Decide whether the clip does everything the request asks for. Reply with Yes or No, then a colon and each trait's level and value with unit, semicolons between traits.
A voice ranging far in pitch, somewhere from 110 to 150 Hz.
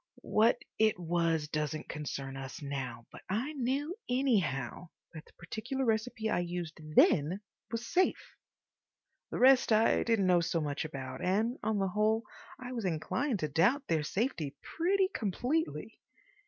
No: wide, 7.8 semitones; high, 195 Hz